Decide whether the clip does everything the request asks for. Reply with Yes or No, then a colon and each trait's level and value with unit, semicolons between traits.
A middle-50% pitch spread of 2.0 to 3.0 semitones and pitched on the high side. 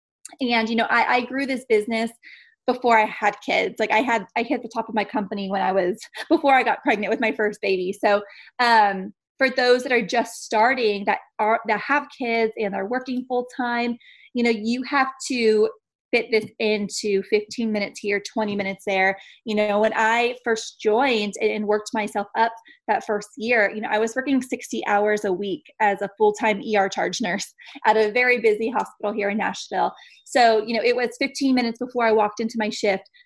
Yes: average, 2.7 semitones; high, 225 Hz